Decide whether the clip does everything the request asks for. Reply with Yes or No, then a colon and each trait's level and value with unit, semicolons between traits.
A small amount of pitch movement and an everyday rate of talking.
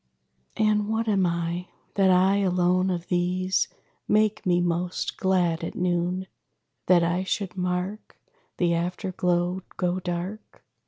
No: narrow, 1.4 semitones; slow, 130 wpm